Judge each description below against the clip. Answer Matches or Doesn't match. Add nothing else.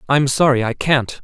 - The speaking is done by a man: Matches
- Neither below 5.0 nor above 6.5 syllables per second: Doesn't match